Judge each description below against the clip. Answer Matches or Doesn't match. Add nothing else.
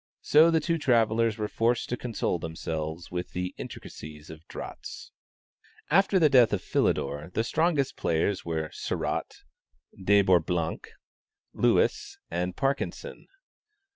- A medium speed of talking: Doesn't match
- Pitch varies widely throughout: Matches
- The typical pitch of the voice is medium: Doesn't match